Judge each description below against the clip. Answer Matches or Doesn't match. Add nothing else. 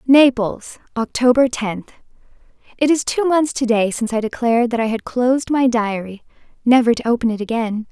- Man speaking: Doesn't match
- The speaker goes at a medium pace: Matches